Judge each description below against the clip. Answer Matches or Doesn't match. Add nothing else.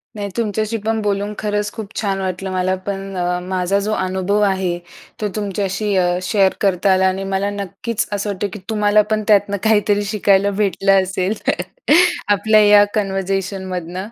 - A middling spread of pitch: Doesn't match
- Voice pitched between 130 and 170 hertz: Doesn't match